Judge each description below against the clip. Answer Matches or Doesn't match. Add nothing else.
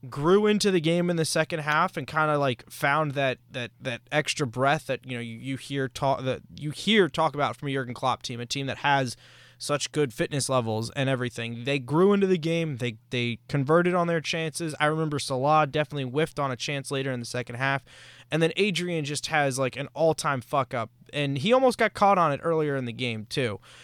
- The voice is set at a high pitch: Doesn't match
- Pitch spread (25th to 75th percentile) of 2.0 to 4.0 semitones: Matches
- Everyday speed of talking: Doesn't match